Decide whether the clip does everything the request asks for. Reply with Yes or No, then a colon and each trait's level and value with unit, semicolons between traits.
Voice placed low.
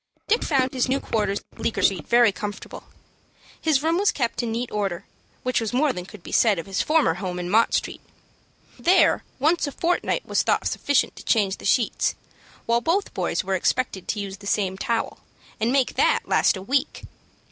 No: high, 230 Hz